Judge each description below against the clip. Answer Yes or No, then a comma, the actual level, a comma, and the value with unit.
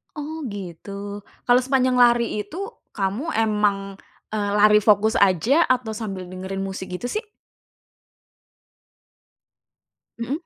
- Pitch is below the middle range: No, high, 210 Hz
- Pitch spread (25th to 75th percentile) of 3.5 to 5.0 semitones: Yes, average, 3.9 semitones